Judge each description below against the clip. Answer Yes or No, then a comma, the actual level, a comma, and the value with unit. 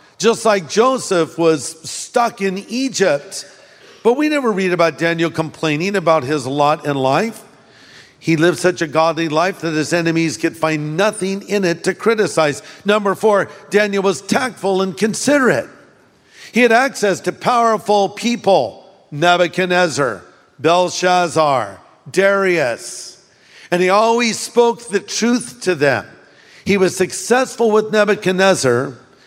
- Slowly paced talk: Yes, slow, 130 wpm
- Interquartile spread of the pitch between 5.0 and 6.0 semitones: No, average, 4.5 semitones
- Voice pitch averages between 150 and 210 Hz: Yes, high, 190 Hz